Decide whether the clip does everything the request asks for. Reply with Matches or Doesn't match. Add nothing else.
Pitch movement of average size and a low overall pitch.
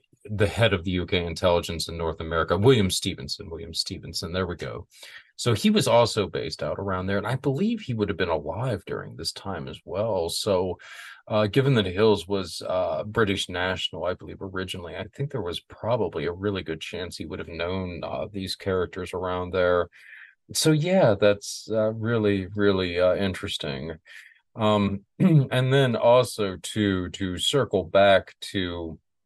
Matches